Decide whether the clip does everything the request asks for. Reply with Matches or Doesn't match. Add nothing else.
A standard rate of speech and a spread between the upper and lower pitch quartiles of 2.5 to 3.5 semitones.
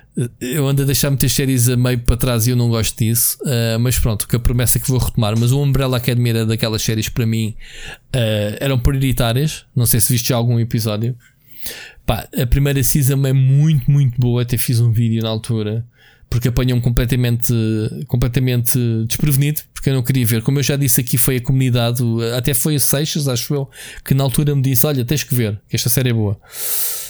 Doesn't match